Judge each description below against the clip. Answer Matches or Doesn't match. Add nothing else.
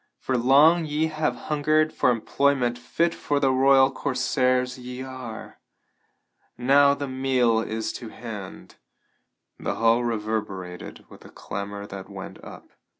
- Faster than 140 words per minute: Doesn't match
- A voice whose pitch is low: Matches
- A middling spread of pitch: Matches